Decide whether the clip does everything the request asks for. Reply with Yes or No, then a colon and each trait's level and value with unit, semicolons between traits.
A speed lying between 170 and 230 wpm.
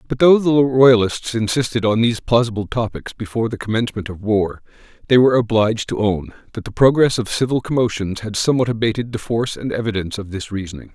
Yes: average, 190 wpm